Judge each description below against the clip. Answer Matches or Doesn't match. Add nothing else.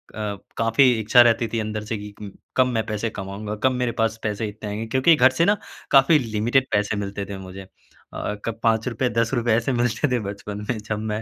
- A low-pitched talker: Matches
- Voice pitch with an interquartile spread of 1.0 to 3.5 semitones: Matches